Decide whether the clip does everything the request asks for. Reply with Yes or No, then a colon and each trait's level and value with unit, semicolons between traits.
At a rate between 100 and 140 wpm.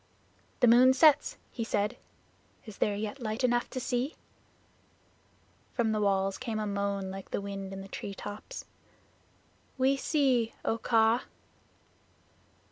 Yes: slow, 135 wpm